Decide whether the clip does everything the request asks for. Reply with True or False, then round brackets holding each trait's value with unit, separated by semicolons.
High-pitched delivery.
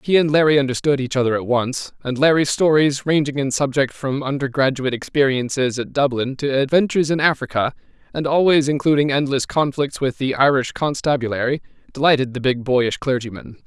False (135 Hz)